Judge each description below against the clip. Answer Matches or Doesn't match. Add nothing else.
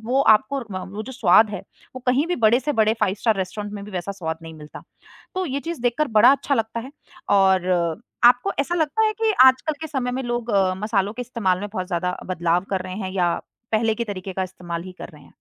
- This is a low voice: Doesn't match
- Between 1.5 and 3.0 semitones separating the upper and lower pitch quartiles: Doesn't match